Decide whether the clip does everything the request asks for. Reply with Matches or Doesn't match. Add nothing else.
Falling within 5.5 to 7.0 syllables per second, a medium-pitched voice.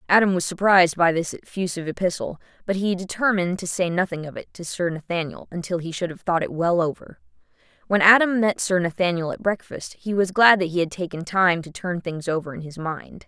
Matches